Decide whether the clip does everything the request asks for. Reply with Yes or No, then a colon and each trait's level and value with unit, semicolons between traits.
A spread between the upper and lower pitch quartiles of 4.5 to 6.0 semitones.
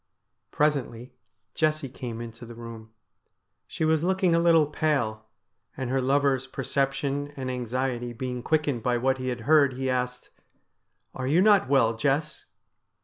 No: average, 3.4 semitones